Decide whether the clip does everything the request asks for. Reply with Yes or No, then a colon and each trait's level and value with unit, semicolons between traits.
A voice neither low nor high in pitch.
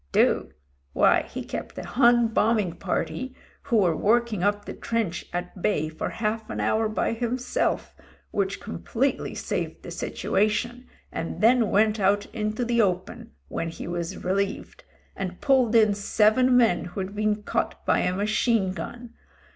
No: high, 215 Hz